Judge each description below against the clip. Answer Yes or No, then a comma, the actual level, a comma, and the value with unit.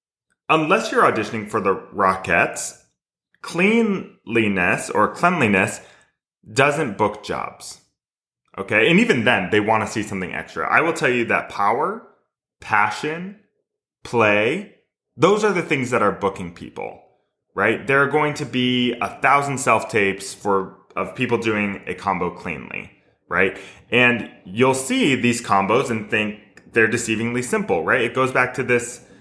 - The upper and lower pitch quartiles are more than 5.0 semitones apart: Yes, wide, 5.4 semitones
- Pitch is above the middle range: No, low, 120 Hz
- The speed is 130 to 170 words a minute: Yes, average, 150 wpm